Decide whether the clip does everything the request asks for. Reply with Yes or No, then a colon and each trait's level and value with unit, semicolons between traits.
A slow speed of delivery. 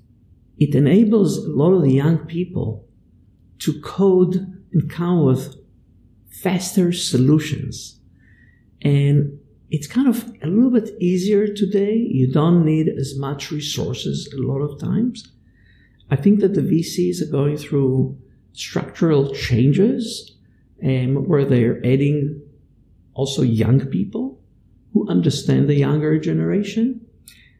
Yes: slow, 125 wpm